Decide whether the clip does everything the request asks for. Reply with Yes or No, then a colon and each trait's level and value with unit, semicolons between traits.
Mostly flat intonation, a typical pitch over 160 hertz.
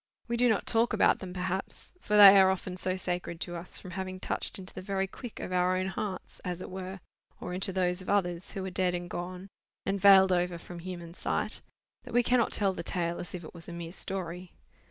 Yes: narrow, 1.4 semitones; medium, 185 Hz